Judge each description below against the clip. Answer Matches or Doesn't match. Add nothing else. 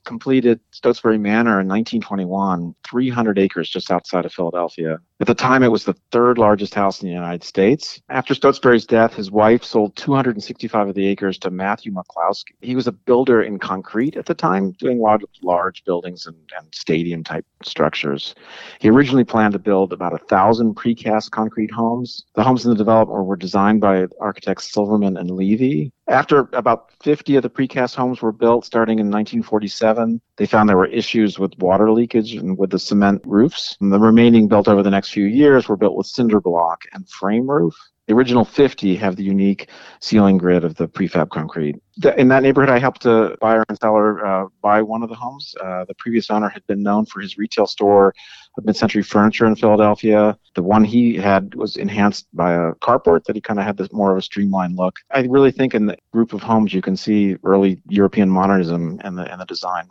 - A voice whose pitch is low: Matches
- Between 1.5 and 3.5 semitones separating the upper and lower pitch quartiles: Matches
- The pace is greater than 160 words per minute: Matches